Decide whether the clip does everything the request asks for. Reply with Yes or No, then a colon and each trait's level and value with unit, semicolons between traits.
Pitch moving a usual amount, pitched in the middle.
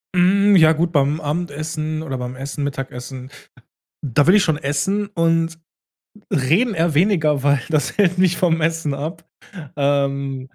Yes: average, 3.4 semitones; medium, 155 Hz